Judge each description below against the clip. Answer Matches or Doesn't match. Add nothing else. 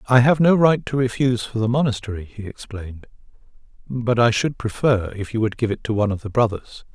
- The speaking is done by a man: Matches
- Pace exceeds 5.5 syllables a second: Matches